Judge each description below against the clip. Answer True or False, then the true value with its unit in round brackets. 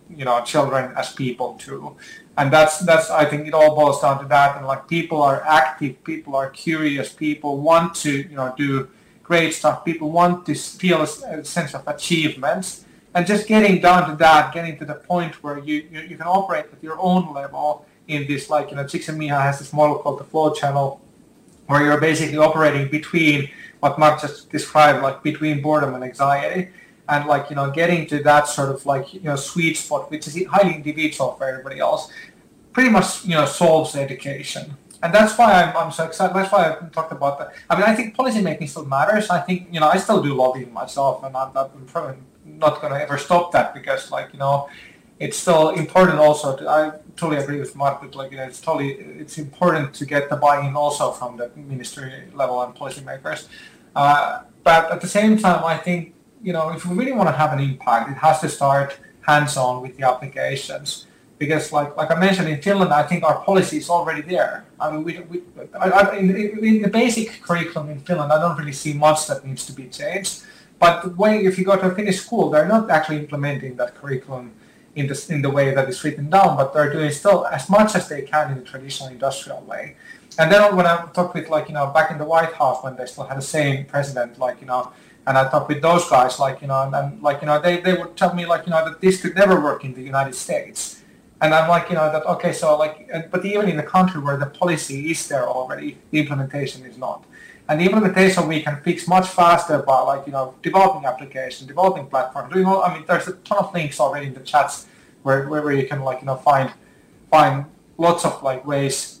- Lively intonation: False (3.8 semitones)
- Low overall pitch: False (155 Hz)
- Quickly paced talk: True (225 wpm)